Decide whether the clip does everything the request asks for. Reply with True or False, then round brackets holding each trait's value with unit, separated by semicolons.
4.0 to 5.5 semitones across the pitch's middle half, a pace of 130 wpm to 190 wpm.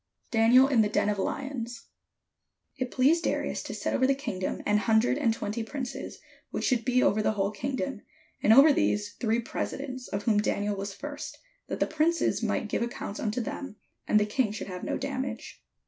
False (4.3 semitones; 200 wpm)